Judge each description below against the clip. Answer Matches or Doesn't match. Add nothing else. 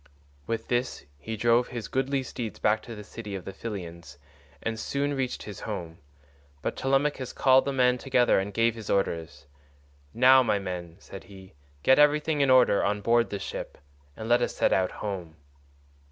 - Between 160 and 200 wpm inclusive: Matches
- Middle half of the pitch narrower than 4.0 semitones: Doesn't match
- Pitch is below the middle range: Matches